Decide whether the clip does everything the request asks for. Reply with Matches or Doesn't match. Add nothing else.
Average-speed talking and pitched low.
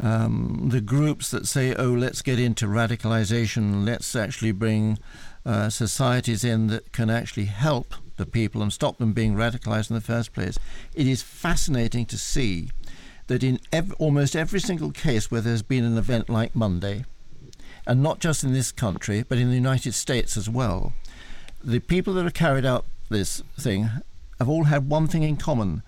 Matches